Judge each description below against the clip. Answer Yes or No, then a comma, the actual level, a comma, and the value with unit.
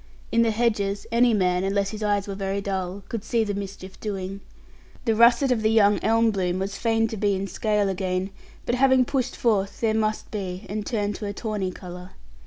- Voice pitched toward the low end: No, high, 205 Hz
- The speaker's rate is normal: No, fast, 210 wpm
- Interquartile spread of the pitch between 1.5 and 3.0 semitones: Yes, narrow, 2.5 semitones